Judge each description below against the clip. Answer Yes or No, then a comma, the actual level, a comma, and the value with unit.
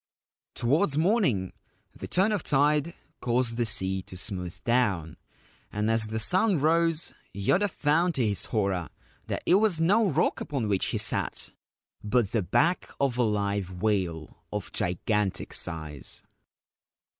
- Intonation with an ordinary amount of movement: No, wide, 8.7 semitones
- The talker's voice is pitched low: Yes, low, 115 Hz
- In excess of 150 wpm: No, average, 145 wpm